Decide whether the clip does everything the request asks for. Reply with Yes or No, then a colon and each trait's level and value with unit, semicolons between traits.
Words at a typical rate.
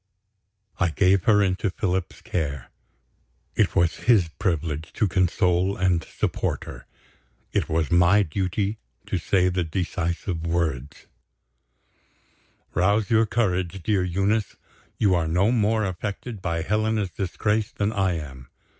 No: slow, 130 wpm